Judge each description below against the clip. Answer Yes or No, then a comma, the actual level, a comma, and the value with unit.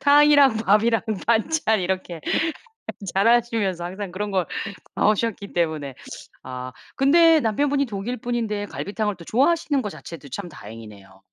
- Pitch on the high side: Yes, high, 210 Hz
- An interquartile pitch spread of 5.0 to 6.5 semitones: Yes, wide, 5.5 semitones